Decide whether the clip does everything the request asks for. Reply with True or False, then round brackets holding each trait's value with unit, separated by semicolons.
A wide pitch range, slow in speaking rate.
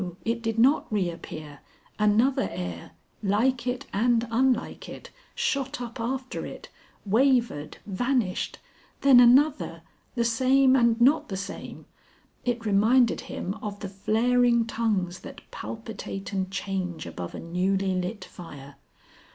False (4.5 semitones; 125 wpm)